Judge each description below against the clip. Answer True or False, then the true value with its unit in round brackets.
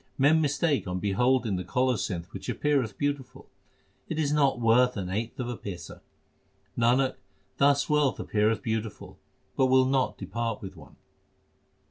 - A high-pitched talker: False (125 Hz)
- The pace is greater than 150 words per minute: False (145 wpm)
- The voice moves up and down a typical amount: True (4.6 semitones)